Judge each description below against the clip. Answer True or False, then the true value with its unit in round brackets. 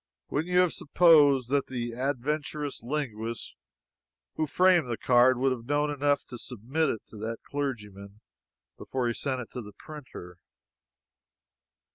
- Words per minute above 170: False (145 wpm)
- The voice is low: True (130 Hz)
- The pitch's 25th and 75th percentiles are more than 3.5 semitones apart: True (3.9 semitones)